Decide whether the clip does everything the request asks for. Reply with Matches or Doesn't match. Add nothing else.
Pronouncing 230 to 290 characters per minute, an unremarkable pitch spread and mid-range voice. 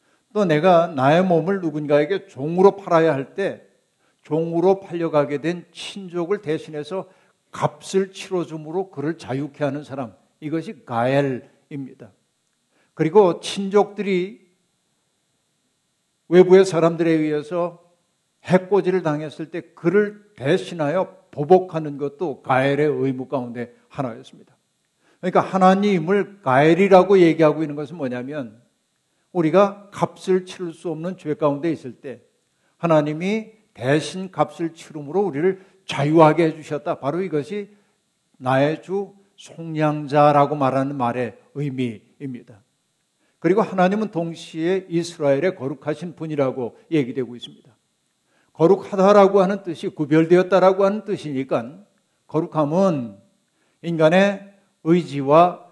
Matches